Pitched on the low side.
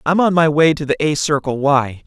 No: medium, 150 Hz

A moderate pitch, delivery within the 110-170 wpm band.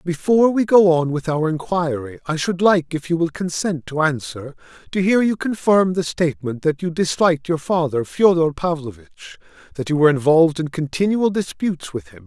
No: medium, 165 Hz; average, 185 wpm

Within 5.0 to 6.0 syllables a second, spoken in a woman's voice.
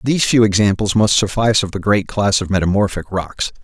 No: 5.8 syllables/s; male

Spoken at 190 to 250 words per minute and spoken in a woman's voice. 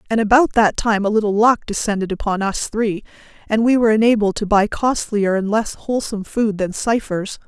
Yes: average, 195 wpm; female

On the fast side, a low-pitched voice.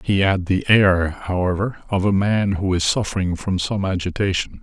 No: average, 180 wpm; very low, 95 Hz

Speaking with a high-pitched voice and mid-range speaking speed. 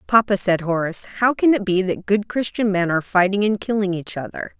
No: high, 200 Hz; fast, 220 wpm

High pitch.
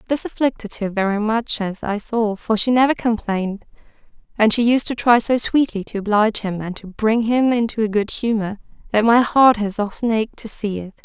Yes: high, 220 Hz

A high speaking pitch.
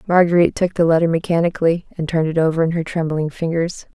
No: medium, 165 Hz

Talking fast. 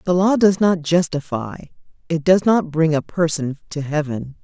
No: average, 175 wpm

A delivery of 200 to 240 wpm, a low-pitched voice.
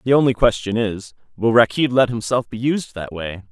Yes: fast, 205 wpm; low, 110 Hz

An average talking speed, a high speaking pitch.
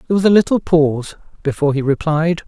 No: average, 195 wpm; medium, 160 Hz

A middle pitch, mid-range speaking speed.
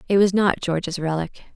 Yes: medium, 180 Hz; average, 195 wpm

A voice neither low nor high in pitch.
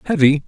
Yes: medium, 155 Hz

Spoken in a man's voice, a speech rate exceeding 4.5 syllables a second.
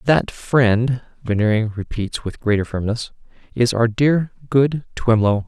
No: male; 4.1 syllables/s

